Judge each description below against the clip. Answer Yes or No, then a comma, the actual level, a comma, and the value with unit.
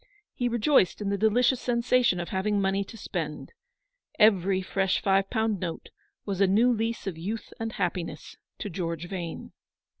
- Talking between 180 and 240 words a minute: No, average, 160 wpm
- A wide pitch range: No, average, 3.6 semitones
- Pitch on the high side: Yes, high, 195 Hz